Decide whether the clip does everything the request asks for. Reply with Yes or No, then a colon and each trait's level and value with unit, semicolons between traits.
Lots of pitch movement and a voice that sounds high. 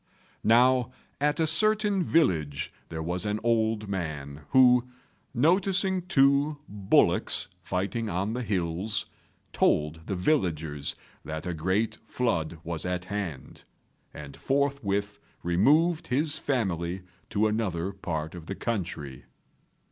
No: wide, 7.5 semitones; low, 105 Hz